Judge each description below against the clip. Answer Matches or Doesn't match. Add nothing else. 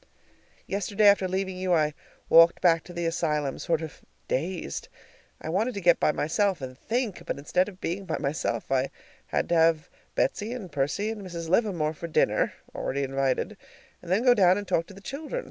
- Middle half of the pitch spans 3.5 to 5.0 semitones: Matches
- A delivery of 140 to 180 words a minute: Doesn't match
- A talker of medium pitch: Matches